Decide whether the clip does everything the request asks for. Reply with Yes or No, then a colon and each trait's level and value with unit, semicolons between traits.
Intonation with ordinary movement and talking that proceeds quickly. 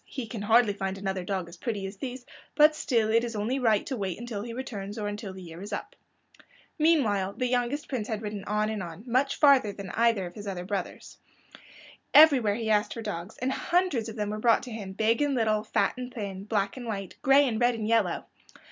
Yes: average, 3.5 semitones; fast, 230 wpm